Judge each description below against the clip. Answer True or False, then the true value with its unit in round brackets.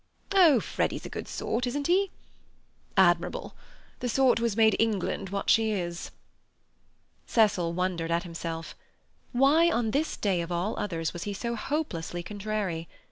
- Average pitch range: False (6.1 semitones)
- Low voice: False (210 Hz)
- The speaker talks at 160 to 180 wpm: False (150 wpm)